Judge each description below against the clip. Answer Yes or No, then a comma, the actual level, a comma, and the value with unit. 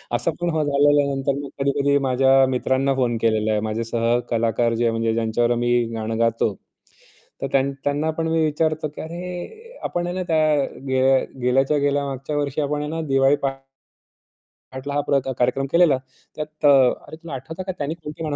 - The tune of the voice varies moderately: Yes, average, 3.6 semitones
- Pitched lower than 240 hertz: Yes, medium, 140 Hz